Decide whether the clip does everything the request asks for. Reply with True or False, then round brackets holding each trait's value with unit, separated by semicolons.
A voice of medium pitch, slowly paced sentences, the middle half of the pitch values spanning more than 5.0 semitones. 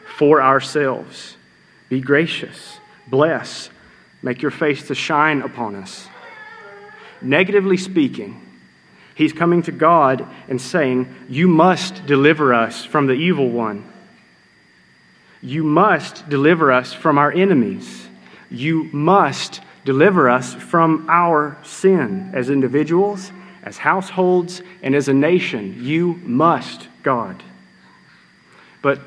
True (150 Hz; 110 wpm; 5.5 semitones)